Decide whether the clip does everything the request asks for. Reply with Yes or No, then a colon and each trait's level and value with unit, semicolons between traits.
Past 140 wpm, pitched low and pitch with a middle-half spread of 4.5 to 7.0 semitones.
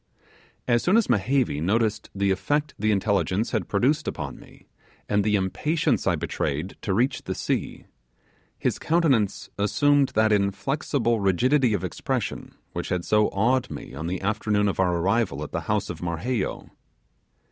Yes: average, 160 wpm; low, 105 Hz; average, 4.9 semitones